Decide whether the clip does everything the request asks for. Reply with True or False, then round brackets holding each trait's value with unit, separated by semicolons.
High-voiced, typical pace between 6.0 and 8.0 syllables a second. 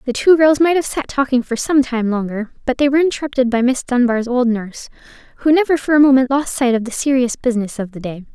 True (255 Hz; 6.3 syllables/s)